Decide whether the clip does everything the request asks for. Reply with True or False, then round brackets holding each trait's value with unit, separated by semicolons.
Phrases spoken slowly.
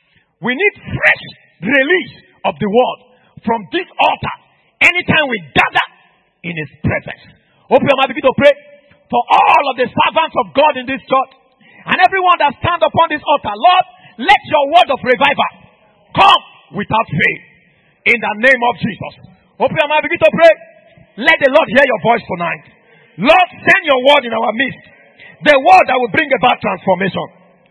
False (170 wpm)